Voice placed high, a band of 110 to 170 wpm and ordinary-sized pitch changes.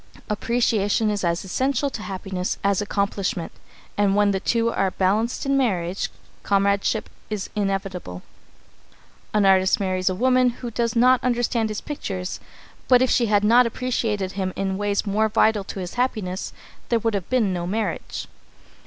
Yes: high, 205 Hz; average, 160 wpm; average, 3.4 semitones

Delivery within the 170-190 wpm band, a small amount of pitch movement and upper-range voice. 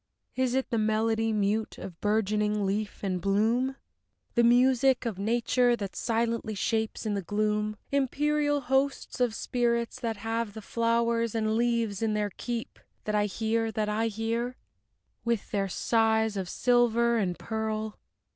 No: average, 155 wpm; narrow, 1.9 semitones; high, 225 Hz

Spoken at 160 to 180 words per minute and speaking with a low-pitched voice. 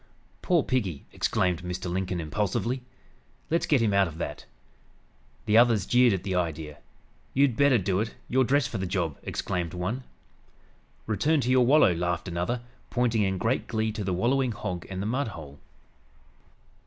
Yes: average, 165 wpm; low, 105 Hz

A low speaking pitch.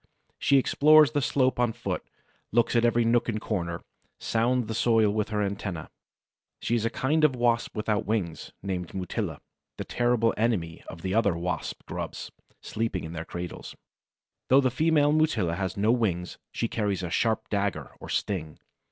Yes: low, 110 Hz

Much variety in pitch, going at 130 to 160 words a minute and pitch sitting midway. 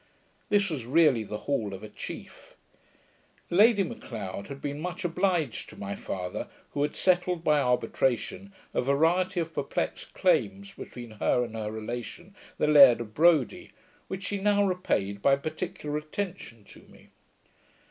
Yes: wide, 7.6 semitones; average, 150 wpm; medium, 150 Hz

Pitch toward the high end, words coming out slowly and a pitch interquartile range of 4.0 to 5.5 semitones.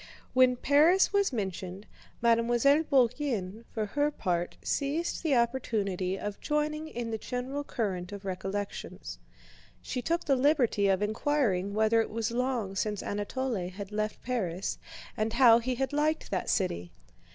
No: high, 230 Hz; average, 145 wpm; average, 5.2 semitones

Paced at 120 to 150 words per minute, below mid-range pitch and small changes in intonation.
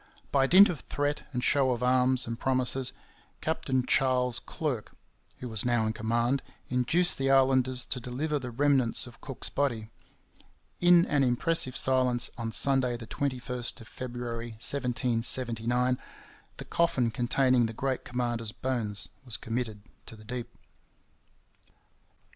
Yes: slow, 135 wpm; low, 125 Hz; narrow, 2.2 semitones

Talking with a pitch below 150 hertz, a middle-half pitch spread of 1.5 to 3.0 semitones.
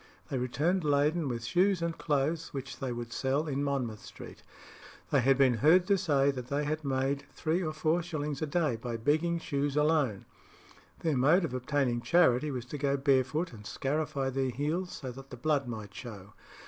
No: medium, 140 Hz; average, 3.5 semitones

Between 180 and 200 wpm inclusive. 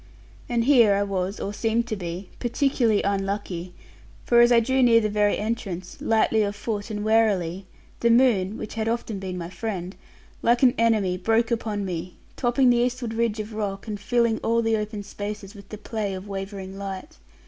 Yes: average, 190 wpm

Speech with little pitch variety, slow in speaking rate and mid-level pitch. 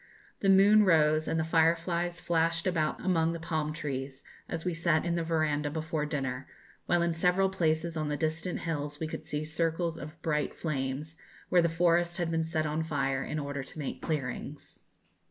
No: narrow, 2.1 semitones; average, 190 wpm; medium, 160 Hz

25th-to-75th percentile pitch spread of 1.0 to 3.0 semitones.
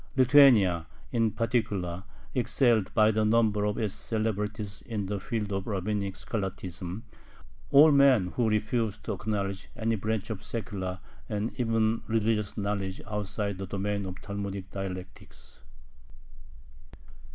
Yes: narrow, 2.4 semitones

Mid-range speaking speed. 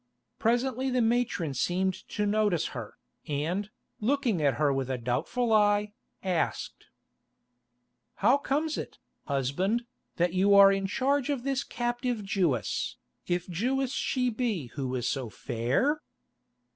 No: slow, 130 wpm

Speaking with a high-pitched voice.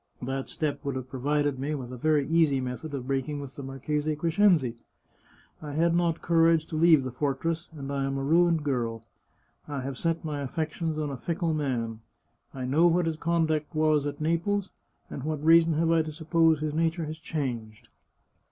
No: medium, 150 Hz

